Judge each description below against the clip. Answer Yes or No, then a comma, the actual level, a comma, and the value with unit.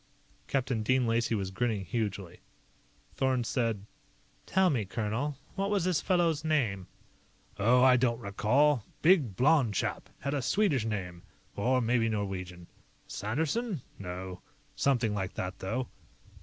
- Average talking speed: No, slow, 130 wpm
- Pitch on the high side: No, low, 120 Hz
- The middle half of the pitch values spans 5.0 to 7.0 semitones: Yes, wide, 5.6 semitones